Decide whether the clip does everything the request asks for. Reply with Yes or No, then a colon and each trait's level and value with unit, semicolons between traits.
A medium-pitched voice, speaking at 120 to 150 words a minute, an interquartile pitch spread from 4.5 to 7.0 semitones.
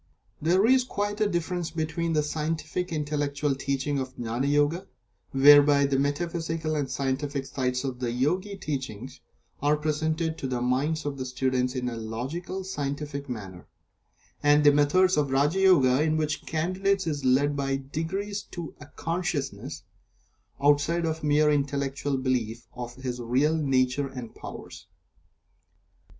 No: medium, 145 Hz; average, 145 wpm; average, 3.4 semitones